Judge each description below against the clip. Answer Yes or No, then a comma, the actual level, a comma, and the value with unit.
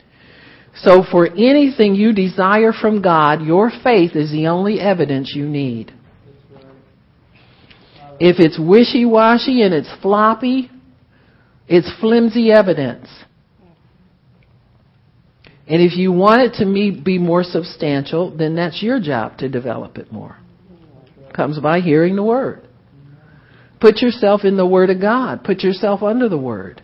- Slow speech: Yes, slow, 130 wpm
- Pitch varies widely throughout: Yes, wide, 6.4 semitones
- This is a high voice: No, medium, 180 Hz